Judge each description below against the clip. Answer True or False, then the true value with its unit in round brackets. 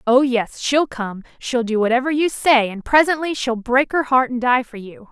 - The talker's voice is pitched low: False (250 Hz)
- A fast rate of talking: True (225 wpm)